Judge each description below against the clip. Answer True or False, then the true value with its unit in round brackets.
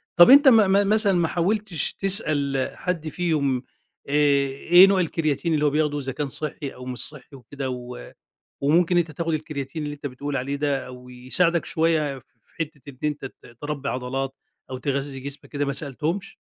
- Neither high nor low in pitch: True (145 Hz)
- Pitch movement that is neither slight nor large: True (3.6 semitones)